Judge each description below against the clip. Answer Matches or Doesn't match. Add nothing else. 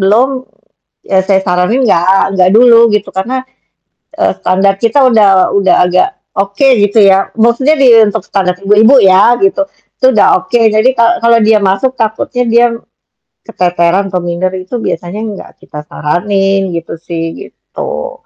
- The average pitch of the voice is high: Matches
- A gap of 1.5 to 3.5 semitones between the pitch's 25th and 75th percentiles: Doesn't match